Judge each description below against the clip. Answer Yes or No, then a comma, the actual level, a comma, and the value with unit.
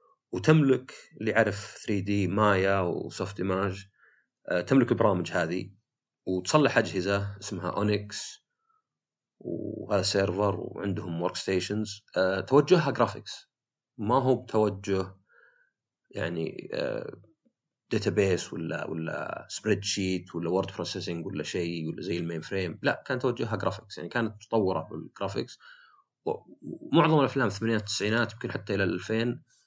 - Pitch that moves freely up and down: No, average, 4.7 semitones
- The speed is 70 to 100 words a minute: No, average, 115 wpm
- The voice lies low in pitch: Yes, low, 105 Hz